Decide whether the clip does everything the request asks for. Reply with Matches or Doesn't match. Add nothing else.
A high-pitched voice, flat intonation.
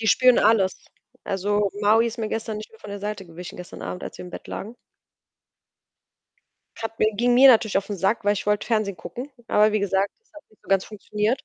Matches